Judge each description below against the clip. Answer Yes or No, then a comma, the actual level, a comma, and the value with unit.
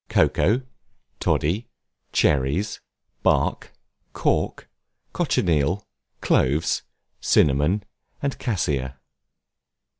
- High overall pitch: No, very low, 80 Hz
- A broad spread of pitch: Yes, wide, 6.7 semitones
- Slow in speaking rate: Yes, slow, 60 wpm